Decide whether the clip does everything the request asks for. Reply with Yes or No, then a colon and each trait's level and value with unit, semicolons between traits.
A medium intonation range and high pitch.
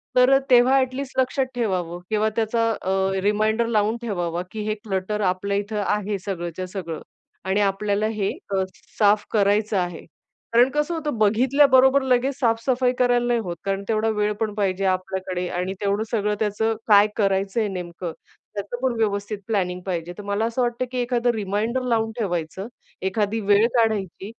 Yes: average, 3.3 semitones; high, 210 Hz